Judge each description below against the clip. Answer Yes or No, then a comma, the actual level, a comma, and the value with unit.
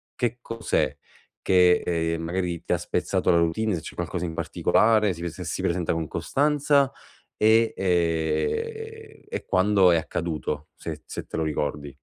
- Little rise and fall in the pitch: No, average, 5.2 semitones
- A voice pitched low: Yes, very low, 90 Hz